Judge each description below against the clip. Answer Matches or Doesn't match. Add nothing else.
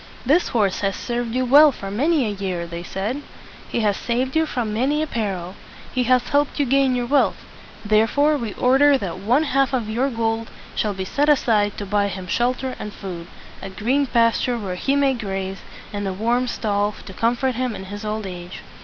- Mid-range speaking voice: Doesn't match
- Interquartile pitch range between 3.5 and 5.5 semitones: Matches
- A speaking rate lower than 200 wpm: Doesn't match